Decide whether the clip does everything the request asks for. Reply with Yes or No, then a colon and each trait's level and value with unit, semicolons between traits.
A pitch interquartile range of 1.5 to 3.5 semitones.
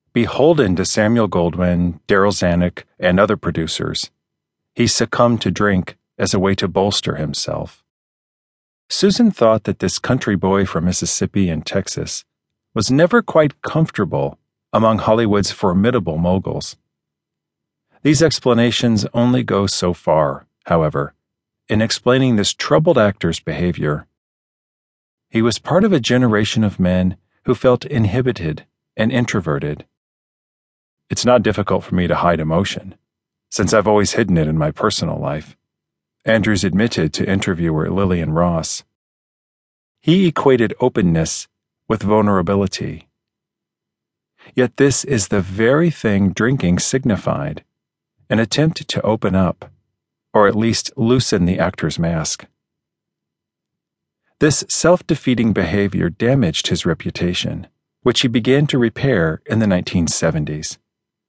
No: wide, 5.5 semitones